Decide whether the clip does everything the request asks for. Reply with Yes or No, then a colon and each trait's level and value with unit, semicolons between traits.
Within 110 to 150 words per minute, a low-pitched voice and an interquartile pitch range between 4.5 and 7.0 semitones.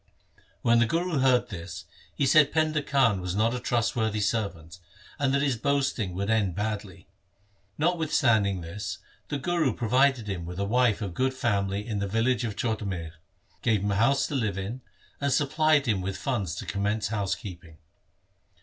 No: average, 175 wpm; low, 110 Hz; average, 5.0 semitones